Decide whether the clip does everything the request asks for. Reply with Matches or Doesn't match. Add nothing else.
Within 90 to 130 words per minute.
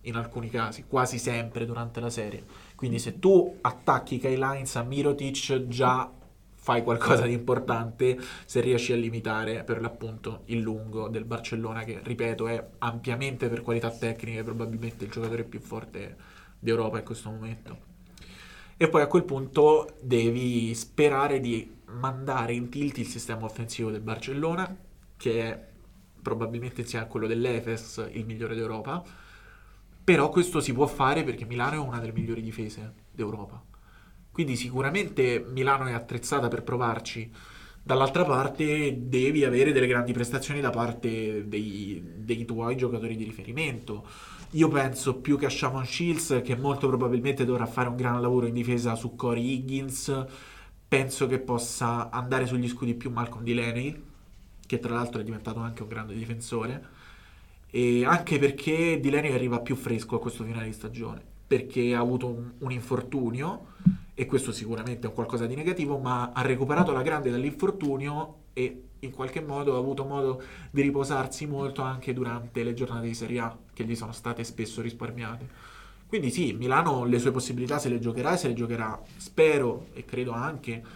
Doesn't match